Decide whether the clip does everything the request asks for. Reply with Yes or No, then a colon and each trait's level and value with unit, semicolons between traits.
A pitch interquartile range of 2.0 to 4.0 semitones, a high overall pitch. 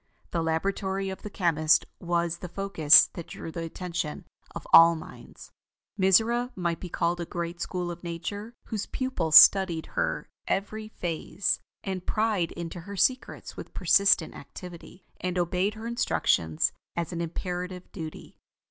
No: average, 2.8 semitones; medium, 180 Hz